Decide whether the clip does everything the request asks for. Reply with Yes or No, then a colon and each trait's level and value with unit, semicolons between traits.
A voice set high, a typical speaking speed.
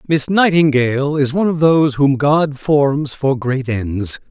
No: medium, 140 Hz; average, 165 wpm